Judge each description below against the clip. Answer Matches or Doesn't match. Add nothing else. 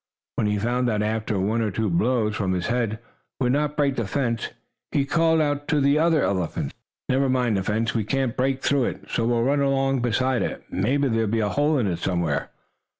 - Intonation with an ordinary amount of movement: Matches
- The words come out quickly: Matches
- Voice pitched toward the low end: Matches